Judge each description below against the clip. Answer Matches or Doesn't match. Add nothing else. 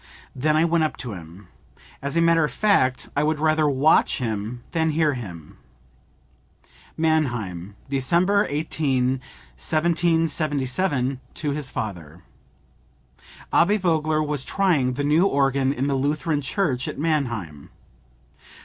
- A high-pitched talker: Doesn't match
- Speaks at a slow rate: Matches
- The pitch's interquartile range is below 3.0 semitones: Doesn't match